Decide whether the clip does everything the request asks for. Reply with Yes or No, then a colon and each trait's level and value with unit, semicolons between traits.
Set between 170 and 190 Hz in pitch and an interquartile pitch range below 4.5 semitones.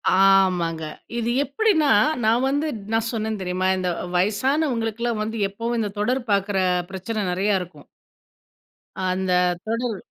No: high, 215 Hz; average, 3.9 semitones